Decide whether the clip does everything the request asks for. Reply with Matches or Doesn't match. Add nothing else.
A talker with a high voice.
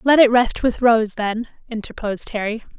Matches